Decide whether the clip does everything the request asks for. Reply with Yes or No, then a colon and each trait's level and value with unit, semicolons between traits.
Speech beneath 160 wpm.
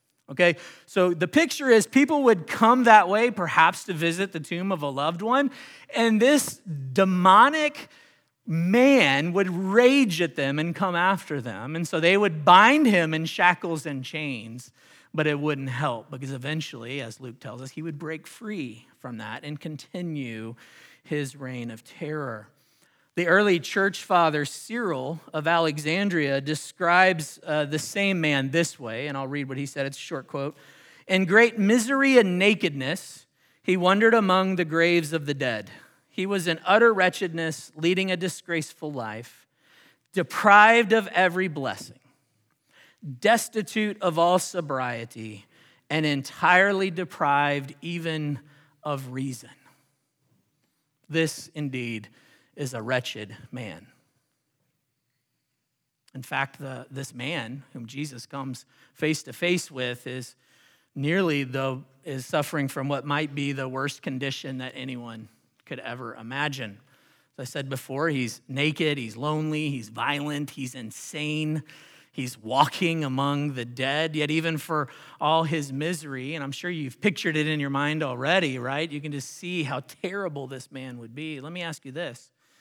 Yes: average, 150 wpm